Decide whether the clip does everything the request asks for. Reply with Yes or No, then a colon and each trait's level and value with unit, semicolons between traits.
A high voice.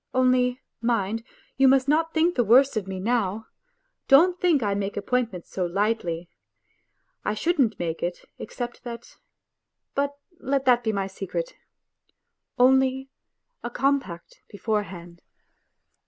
Yes: high, 240 Hz